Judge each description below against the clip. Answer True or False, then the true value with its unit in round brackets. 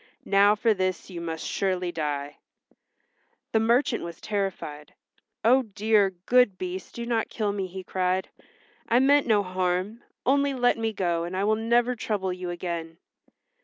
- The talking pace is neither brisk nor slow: True (160 wpm)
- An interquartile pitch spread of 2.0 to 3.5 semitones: False (4.0 semitones)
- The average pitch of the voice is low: False (195 Hz)